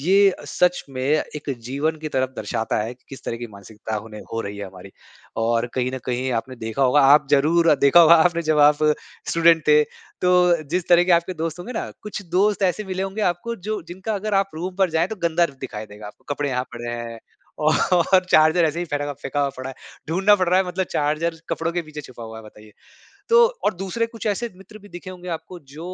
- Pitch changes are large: Yes, wide, 5.8 semitones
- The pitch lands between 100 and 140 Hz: No, medium, 160 Hz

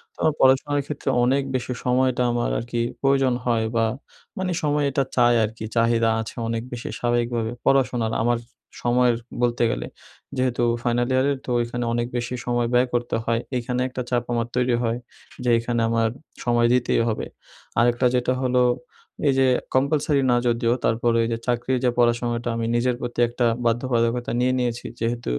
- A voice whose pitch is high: No, low, 120 Hz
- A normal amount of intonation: No, narrow, 1.2 semitones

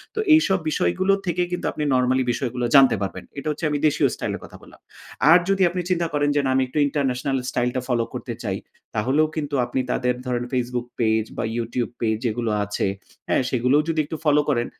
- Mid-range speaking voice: No, low, 130 Hz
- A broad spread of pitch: No, average, 3.8 semitones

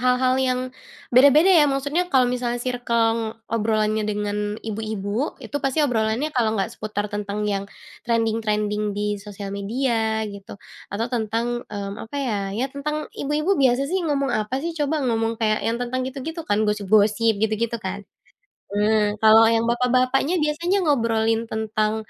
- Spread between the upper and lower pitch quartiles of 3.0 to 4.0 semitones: Yes, average, 3.5 semitones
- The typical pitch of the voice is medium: No, high, 225 Hz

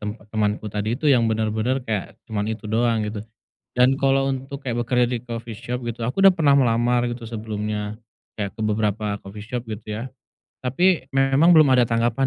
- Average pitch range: Yes, average, 3.2 semitones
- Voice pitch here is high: No, low, 115 Hz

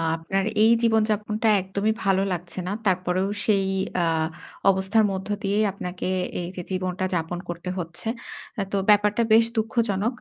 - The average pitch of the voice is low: No, high, 195 Hz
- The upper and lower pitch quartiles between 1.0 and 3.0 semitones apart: Yes, average, 2.7 semitones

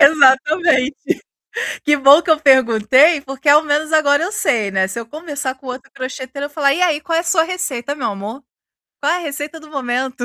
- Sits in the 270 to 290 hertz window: Yes, very high, 285 Hz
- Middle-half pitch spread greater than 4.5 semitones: No, average, 3.1 semitones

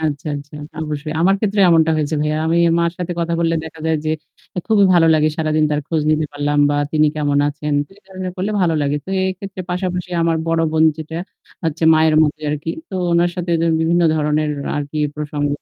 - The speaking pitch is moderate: Yes, medium, 160 Hz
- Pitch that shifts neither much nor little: No, narrow, 2.2 semitones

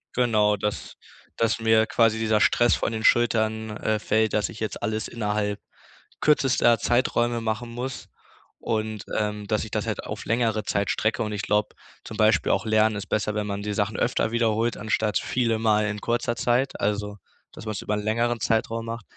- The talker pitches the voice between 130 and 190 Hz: No, low, 110 Hz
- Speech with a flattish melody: Yes, narrow, 1.6 semitones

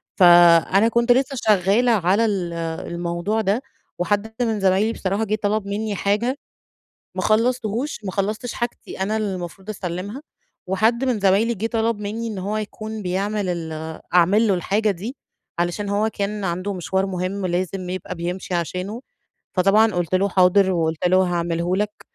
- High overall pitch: Yes, high, 200 Hz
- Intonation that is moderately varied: Yes, average, 3.1 semitones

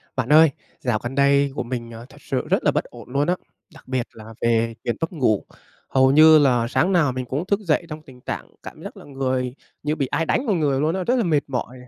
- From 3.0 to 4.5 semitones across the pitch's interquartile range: Yes, average, 3.9 semitones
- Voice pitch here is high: No, medium, 140 Hz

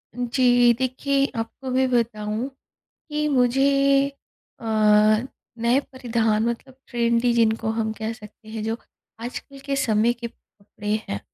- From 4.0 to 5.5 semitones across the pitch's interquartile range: No, average, 2.7 semitones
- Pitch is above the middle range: Yes, high, 235 Hz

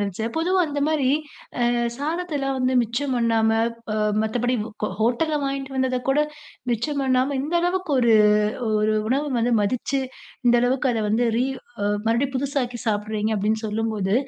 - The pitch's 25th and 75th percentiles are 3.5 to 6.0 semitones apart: Yes, average, 3.9 semitones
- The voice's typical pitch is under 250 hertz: No, very high, 255 Hz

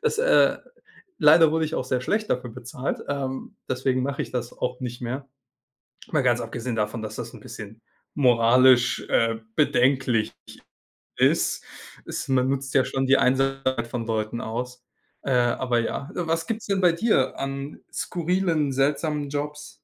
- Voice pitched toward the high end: No, low, 130 Hz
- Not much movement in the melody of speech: No, average, 3.3 semitones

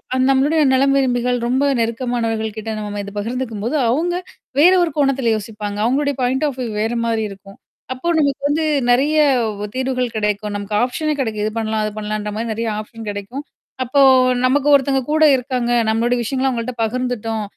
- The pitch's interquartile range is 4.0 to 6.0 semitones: No, average, 3.6 semitones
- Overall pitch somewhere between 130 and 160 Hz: No, high, 245 Hz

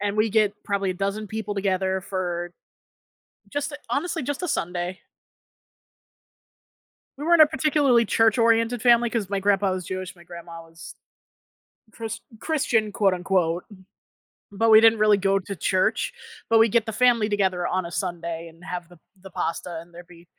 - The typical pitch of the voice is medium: No, high, 200 Hz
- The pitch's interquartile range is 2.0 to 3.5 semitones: No, average, 4.0 semitones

